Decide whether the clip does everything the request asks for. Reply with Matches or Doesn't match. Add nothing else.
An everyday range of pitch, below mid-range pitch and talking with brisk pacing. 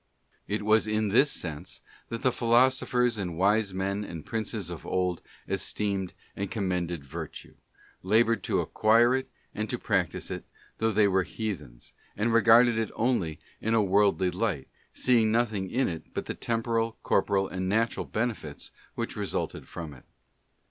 Doesn't match